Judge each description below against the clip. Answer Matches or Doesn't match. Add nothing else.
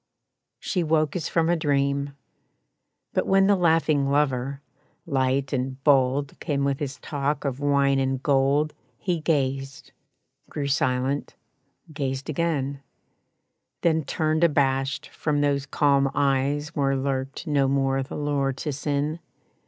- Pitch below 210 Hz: Matches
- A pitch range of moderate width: Doesn't match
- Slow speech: Matches